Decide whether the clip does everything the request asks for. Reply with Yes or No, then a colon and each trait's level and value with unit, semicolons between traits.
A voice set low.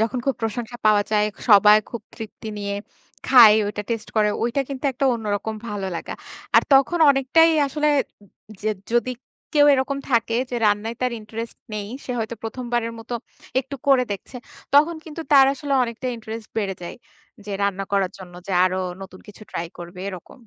No: high, 225 Hz